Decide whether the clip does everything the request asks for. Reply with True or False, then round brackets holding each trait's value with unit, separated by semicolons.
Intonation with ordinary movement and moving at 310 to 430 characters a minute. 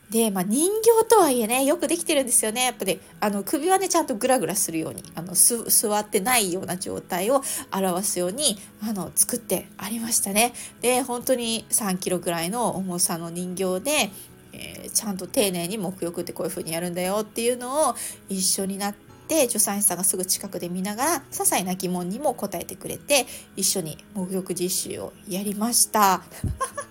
True (5.0 semitones; 370 characters per minute)